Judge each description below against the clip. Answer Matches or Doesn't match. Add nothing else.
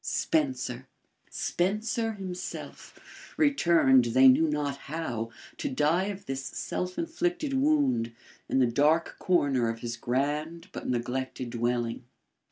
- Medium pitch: Matches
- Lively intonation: Matches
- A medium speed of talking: Doesn't match